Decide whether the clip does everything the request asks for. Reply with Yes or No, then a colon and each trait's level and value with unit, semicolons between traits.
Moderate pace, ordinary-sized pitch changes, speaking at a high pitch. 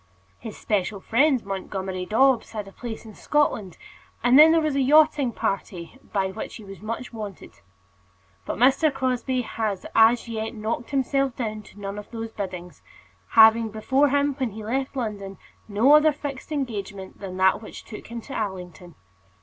Yes: average, 170 wpm; average, 4.9 semitones; high, 225 Hz